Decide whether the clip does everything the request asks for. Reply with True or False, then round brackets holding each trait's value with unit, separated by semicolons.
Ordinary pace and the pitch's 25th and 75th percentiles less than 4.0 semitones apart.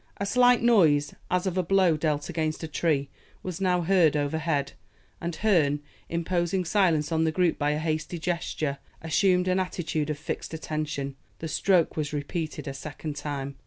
True (170 wpm; 3.4 semitones)